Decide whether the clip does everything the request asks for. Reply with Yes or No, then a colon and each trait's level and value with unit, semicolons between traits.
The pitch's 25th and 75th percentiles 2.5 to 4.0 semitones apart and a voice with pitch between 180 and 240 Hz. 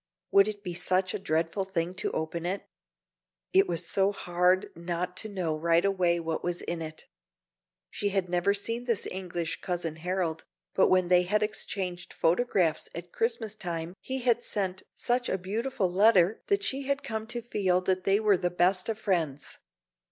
Yes: average, 3.2 semitones; medium, 185 Hz